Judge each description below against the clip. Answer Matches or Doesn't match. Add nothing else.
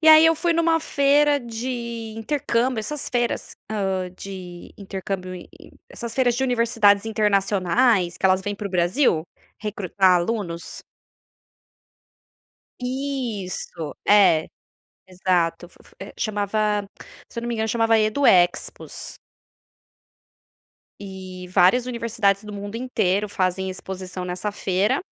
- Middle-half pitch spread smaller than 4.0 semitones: Doesn't match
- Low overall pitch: Doesn't match